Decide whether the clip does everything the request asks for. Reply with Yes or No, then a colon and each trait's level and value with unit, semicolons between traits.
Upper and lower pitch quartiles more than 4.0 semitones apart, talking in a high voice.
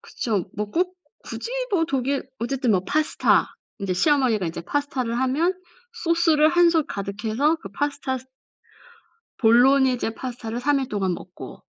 Yes: average, 5.3 semitones; very high, 260 Hz